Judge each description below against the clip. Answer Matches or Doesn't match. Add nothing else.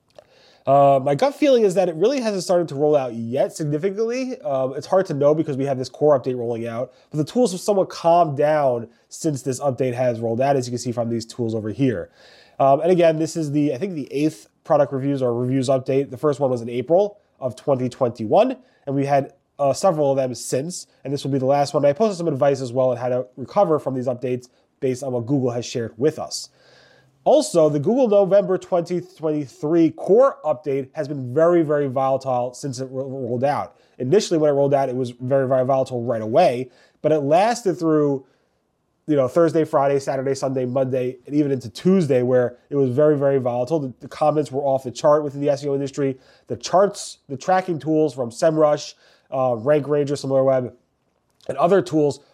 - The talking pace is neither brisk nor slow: Doesn't match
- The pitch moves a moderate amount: Matches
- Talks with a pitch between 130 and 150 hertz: Matches